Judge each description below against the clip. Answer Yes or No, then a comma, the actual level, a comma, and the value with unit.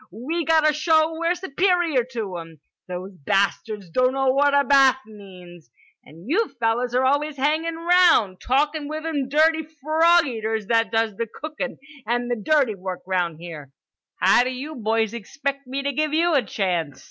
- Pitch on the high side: Yes, very high, 260 Hz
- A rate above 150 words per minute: Yes, average, 165 wpm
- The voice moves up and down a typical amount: No, wide, 6.5 semitones